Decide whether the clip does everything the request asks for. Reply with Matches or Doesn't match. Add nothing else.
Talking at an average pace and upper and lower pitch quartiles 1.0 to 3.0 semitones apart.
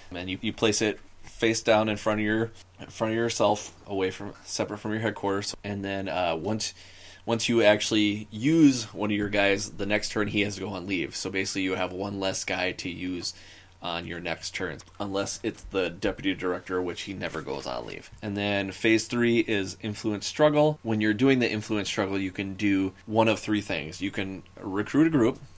Doesn't match